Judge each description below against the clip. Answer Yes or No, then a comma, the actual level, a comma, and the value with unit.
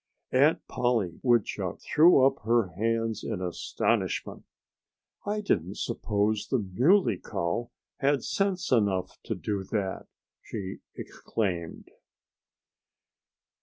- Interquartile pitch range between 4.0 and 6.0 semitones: Yes, average, 5.3 semitones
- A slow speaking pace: Yes, slow, 100 wpm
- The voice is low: Yes, low, 110 Hz